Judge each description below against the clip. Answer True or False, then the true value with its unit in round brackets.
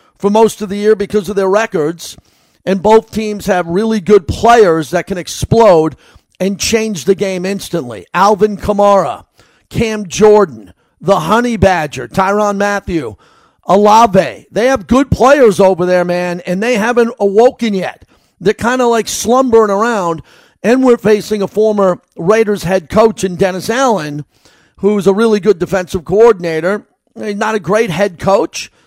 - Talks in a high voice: True (205 Hz)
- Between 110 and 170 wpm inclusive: True (155 wpm)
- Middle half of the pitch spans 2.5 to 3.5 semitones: True (2.8 semitones)